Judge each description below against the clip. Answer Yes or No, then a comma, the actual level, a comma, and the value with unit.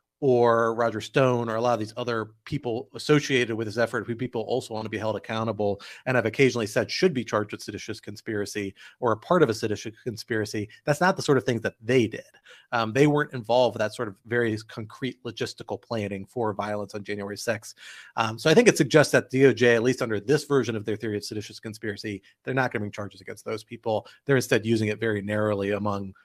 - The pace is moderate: No, fast, 230 wpm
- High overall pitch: No, low, 115 Hz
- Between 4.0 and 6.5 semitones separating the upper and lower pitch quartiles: No, average, 2.9 semitones